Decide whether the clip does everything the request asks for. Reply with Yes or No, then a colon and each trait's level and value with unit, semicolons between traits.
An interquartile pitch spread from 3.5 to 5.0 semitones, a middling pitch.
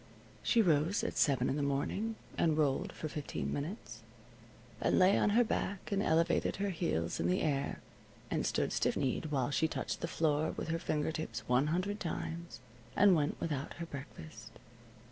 Yes: average, 4.3 semitones; medium, 160 Hz